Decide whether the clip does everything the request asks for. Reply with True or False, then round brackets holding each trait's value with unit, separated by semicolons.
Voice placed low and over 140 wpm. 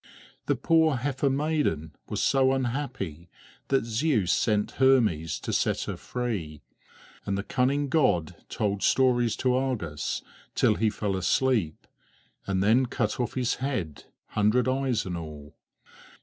False (120 Hz; 135 wpm)